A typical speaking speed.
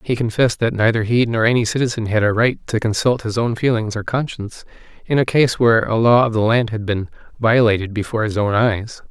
No: fast, 225 wpm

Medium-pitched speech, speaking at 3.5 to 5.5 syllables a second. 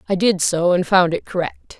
Yes: medium, 180 Hz; 5.0 syllables/s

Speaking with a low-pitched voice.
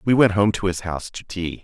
Yes: very low, 95 Hz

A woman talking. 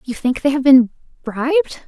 Yes: female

